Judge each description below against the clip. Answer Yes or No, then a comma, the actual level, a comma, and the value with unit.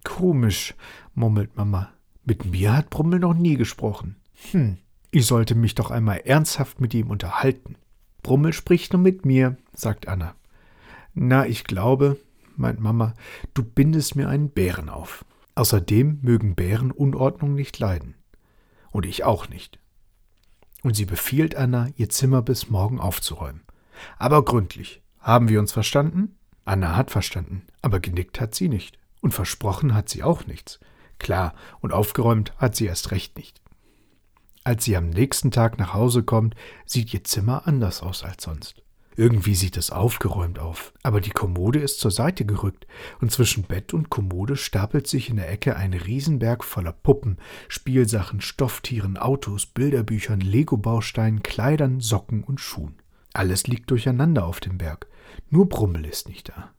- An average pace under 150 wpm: No, average, 155 wpm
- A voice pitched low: Yes, low, 110 Hz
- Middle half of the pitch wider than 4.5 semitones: Yes, average, 5.1 semitones